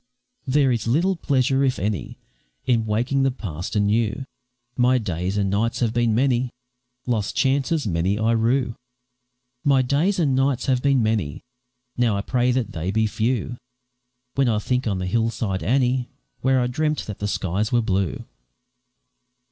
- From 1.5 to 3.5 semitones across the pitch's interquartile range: No, average, 4.0 semitones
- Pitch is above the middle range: No, low, 120 Hz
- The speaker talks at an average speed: Yes, average, 165 wpm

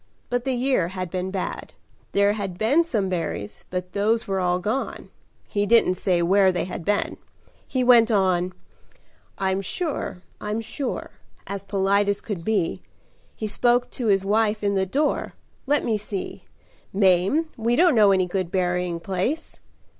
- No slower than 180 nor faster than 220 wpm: No, average, 160 wpm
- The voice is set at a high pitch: Yes, high, 200 Hz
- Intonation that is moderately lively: Yes, average, 3.6 semitones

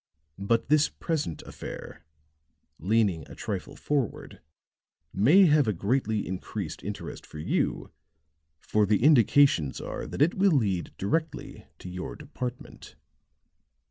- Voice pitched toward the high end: No, low, 110 Hz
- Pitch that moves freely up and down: Yes, wide, 7.2 semitones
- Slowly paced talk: Yes, slow, 120 wpm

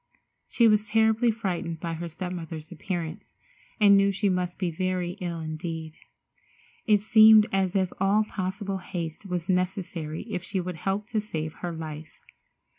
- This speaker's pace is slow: No, average, 160 wpm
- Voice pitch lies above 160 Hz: Yes, medium, 185 Hz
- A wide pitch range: No, average, 3.3 semitones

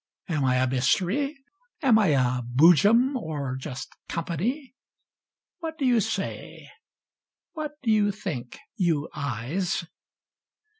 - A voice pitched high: No, medium, 175 Hz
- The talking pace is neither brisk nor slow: No, slow, 120 wpm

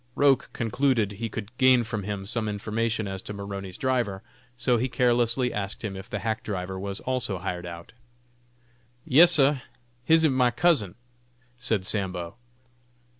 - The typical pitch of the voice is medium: No, low, 110 Hz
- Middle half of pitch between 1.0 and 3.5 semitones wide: No, average, 4.3 semitones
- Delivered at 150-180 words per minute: Yes, average, 155 wpm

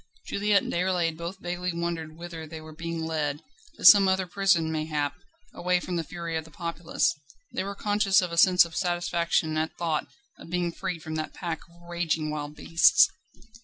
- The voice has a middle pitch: Yes, medium, 170 Hz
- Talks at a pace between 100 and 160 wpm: No, average, 190 wpm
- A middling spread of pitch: No, narrow, 2.0 semitones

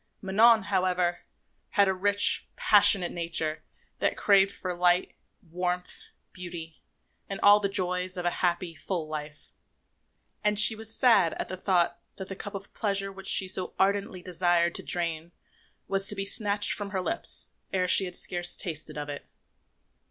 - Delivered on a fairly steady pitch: Yes, narrow, 2.3 semitones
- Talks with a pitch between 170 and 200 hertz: Yes, medium, 185 Hz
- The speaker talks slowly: No, average, 165 wpm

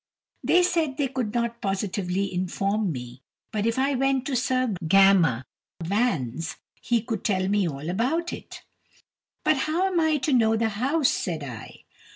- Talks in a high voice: Yes, high, 220 Hz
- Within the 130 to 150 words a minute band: No, average, 165 wpm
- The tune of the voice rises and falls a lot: Yes, wide, 6.1 semitones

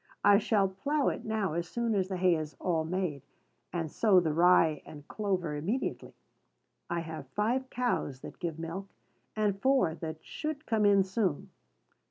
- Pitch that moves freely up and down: No, average, 4.7 semitones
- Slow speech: No, average, 170 wpm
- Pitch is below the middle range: No, medium, 185 Hz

